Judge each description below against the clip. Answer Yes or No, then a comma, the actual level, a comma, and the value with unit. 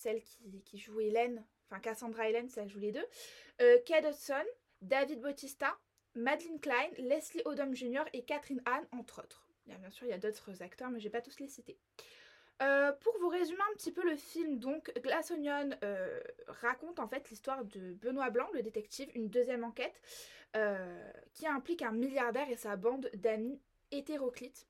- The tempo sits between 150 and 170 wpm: No, average, 195 wpm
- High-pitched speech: Yes, very high, 260 Hz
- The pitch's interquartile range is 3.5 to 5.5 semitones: Yes, average, 4.7 semitones